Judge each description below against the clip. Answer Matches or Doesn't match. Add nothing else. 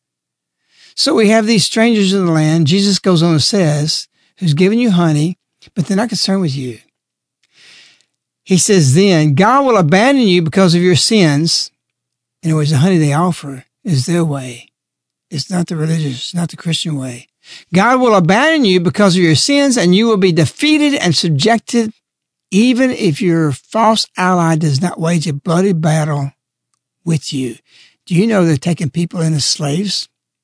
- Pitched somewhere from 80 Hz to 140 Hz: Doesn't match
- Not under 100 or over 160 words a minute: Doesn't match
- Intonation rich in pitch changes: Doesn't match